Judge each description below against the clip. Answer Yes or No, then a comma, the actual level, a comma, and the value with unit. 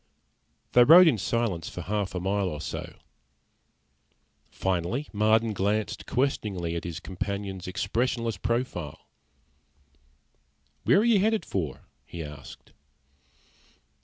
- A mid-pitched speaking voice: No, low, 100 Hz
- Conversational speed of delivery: No, slow, 110 wpm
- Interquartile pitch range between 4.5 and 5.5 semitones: Yes, average, 5.0 semitones